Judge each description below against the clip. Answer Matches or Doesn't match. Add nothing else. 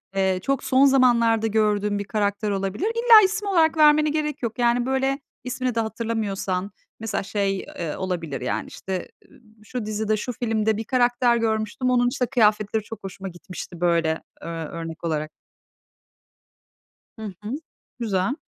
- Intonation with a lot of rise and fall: Doesn't match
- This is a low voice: Doesn't match